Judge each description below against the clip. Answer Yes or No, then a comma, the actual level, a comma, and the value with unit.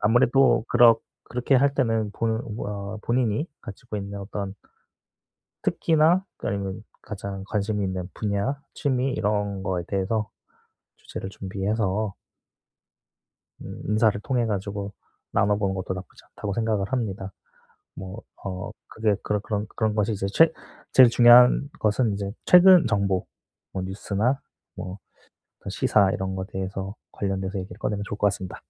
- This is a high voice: No, low, 105 Hz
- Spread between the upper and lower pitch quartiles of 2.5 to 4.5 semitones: Yes, average, 2.9 semitones